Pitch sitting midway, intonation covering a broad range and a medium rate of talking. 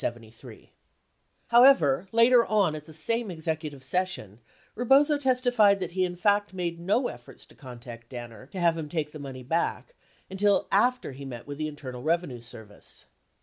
Yes: medium, 165 Hz; wide, 7.6 semitones; average, 165 wpm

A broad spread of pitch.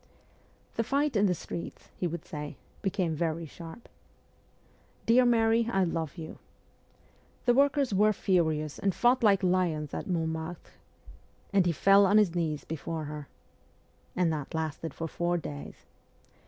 No: average, 4.2 semitones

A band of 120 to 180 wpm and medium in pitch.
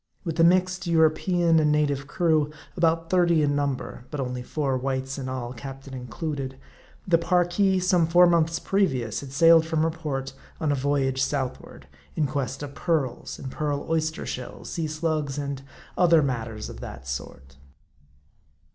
Yes: average, 160 wpm; medium, 150 Hz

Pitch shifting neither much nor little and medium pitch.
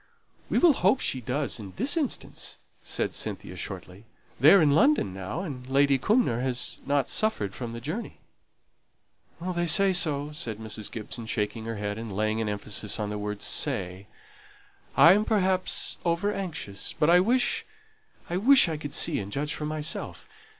No: wide, 9.0 semitones; medium, 145 Hz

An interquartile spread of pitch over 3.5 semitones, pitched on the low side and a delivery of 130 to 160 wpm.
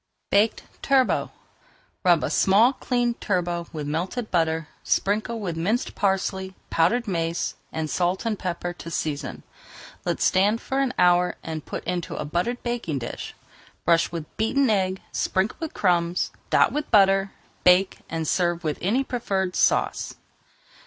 No: average, 4.4 semitones; medium, 185 Hz; average, 145 wpm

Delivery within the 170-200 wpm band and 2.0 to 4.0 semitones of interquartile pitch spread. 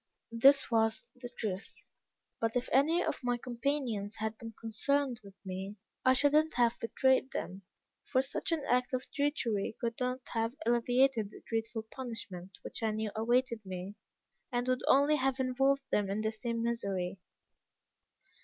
No: average, 160 wpm; average, 3.2 semitones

